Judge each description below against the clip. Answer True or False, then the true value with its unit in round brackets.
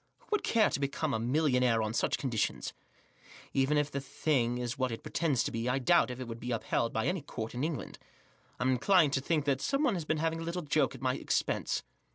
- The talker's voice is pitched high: False (135 Hz)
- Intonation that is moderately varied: True (4.3 semitones)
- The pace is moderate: False (235 wpm)